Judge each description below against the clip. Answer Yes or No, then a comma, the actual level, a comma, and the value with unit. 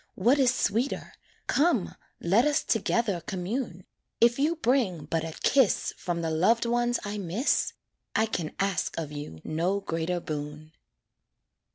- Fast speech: No, average, 145 wpm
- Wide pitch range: Yes, wide, 6.5 semitones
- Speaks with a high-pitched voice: Yes, high, 195 Hz